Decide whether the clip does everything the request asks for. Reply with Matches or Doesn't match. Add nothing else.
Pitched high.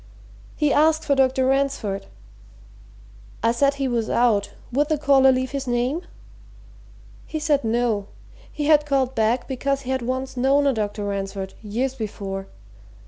Matches